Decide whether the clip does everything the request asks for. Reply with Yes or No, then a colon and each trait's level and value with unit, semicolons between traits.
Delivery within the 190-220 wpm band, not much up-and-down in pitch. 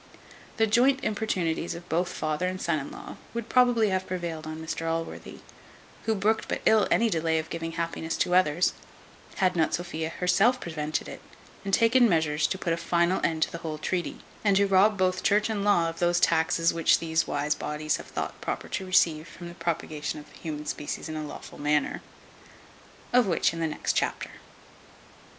No: average, 195 wpm; average, 3.2 semitones